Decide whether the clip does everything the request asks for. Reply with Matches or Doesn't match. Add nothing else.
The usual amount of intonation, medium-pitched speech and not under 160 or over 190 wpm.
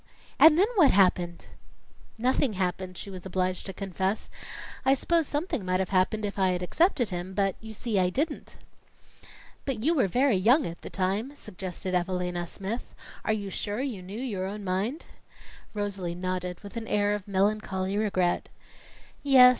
Doesn't match